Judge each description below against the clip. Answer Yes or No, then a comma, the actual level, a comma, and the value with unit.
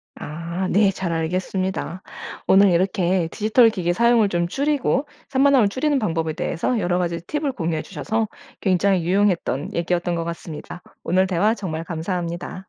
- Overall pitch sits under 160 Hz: No, medium, 185 Hz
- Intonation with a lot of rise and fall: No, average, 3.9 semitones